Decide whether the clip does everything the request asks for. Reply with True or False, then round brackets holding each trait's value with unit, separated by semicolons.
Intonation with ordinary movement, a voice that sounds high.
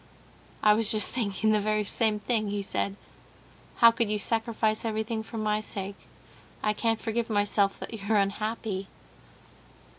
False (1.5 semitones; 215 Hz)